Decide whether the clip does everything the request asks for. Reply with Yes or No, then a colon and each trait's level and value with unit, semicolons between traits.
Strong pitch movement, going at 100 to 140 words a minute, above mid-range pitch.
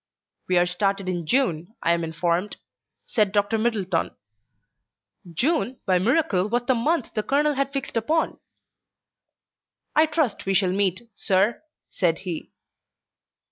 Yes: wide, 5.8 semitones; slow, 135 wpm; high, 205 Hz